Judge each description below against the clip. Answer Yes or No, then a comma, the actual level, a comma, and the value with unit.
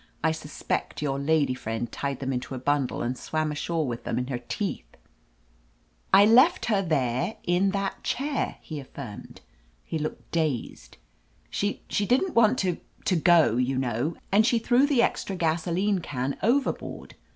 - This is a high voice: No, medium, 160 Hz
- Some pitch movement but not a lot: No, wide, 7.4 semitones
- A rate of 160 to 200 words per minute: Yes, average, 175 wpm